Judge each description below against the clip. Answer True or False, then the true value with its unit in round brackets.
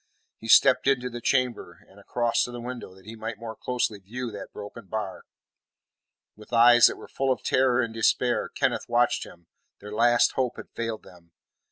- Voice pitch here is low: True (115 Hz)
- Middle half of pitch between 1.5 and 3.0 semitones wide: True (2.7 semitones)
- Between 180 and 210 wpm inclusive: True (190 wpm)